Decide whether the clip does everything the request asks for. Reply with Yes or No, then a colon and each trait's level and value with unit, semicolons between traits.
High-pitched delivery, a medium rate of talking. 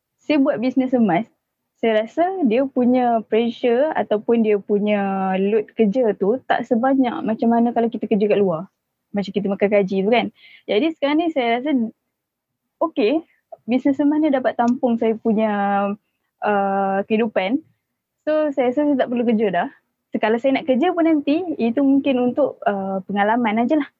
No: high, 235 Hz; fast, 165 wpm